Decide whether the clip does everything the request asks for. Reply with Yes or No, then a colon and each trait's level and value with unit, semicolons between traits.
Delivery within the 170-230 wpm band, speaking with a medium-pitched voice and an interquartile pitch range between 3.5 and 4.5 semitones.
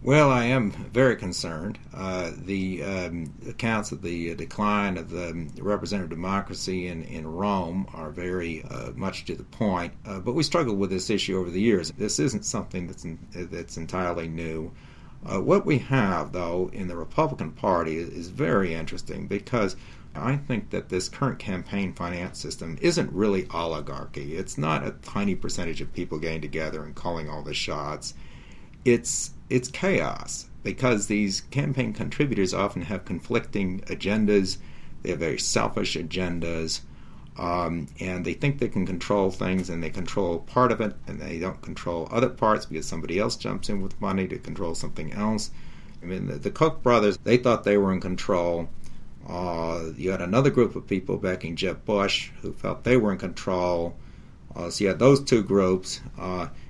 No: average, 175 wpm; very low, 95 Hz; average, 3.8 semitones